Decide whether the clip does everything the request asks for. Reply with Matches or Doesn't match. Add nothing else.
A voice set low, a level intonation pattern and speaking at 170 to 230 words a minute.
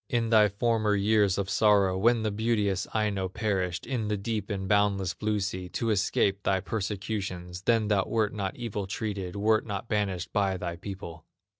Matches